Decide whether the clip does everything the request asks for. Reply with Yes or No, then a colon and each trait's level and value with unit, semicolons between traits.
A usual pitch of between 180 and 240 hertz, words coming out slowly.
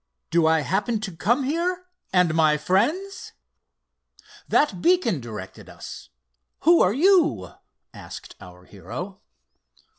Yes: high, 190 Hz; slow, 110 wpm